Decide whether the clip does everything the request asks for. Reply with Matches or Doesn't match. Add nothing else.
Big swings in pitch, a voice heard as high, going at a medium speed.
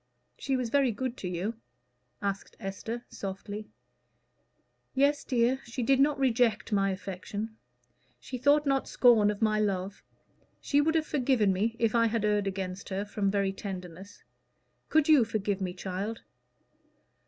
Doesn't match